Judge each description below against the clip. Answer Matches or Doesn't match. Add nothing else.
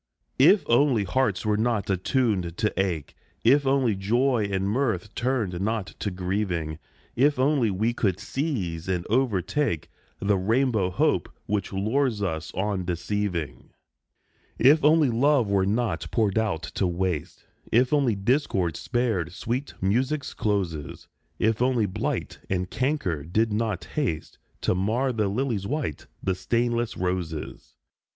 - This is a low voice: Matches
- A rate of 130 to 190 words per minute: Matches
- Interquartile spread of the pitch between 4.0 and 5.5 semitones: Matches